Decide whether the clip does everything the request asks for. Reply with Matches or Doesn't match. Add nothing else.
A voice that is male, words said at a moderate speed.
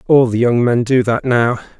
Doesn't match